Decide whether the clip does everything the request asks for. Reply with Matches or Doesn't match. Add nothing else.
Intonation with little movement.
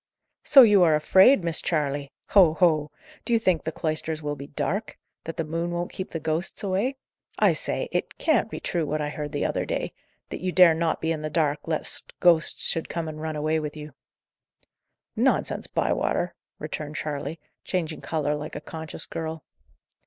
Matches